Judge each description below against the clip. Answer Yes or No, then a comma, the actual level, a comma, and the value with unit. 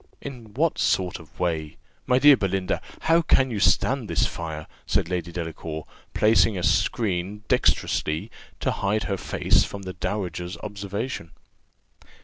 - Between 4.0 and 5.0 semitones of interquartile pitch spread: Yes, average, 4.4 semitones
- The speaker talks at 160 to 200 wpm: No, average, 140 wpm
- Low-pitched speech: Yes, low, 100 Hz